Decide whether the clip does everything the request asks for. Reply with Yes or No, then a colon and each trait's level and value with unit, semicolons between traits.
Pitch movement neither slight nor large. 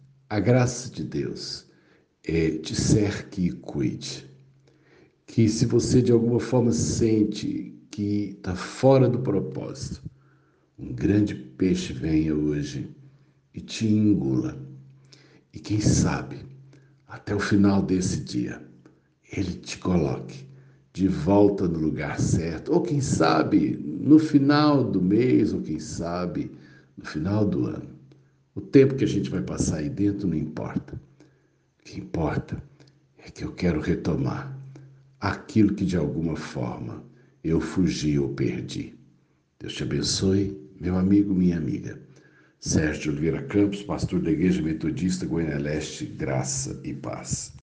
No: wide, 7.3 semitones